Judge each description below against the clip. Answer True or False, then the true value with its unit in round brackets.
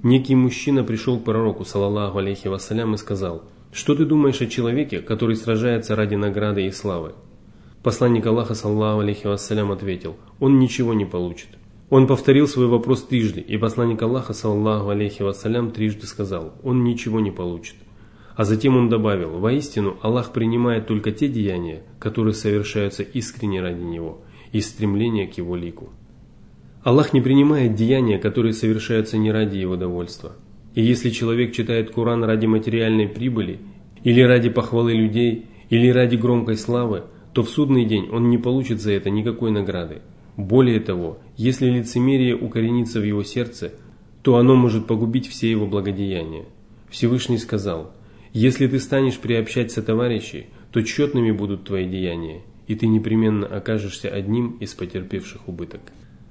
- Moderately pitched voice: False (110 Hz)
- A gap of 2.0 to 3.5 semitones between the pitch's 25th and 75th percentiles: True (2.8 semitones)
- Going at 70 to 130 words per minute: False (150 wpm)